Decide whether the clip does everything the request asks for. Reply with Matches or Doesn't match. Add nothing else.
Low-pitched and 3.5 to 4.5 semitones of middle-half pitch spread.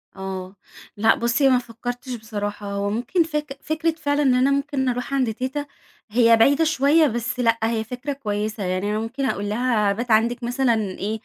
Doesn't match